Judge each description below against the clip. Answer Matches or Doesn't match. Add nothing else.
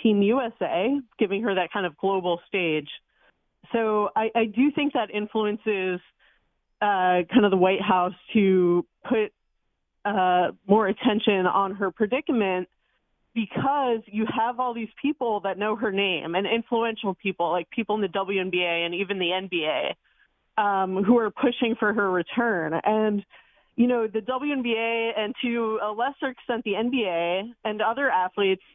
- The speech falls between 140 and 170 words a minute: Matches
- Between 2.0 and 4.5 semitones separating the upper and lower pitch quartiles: Matches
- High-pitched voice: Matches